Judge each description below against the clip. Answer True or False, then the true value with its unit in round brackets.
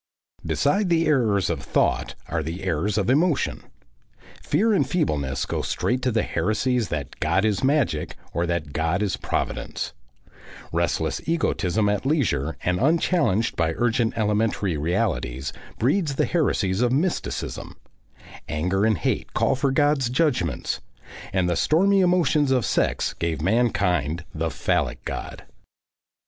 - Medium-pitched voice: False (110 Hz)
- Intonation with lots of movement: True (8.4 semitones)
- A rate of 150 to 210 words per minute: False (135 wpm)